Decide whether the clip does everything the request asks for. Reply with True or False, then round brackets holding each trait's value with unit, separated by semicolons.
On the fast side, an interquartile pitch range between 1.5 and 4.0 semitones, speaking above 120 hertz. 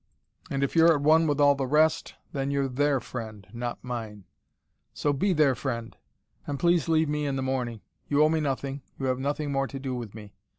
True (215 wpm; 2.9 semitones; 140 Hz)